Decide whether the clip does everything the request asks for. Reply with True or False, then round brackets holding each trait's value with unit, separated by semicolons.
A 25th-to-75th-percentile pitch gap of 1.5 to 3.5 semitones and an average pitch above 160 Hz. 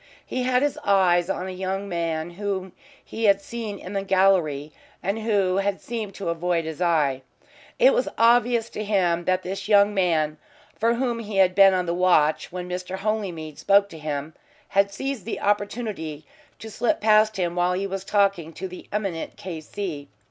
True (3.1 semitones; 190 Hz)